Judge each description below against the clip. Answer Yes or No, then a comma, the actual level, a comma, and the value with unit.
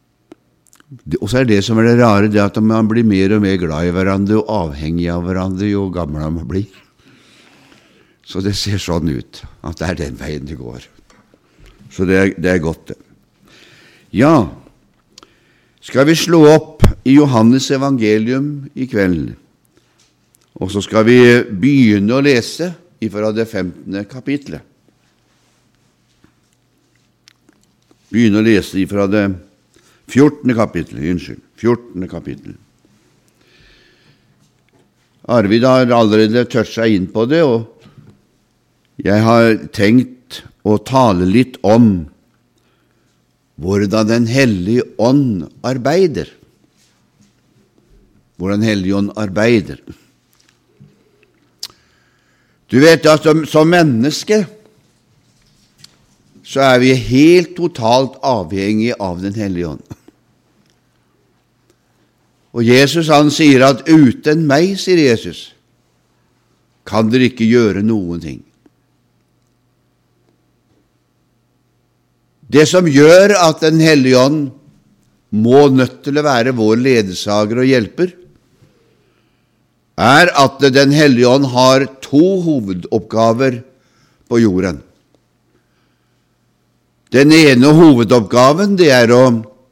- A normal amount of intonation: No, wide, 5.7 semitones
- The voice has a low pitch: Yes, low, 115 Hz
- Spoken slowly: Yes, slow, 110 wpm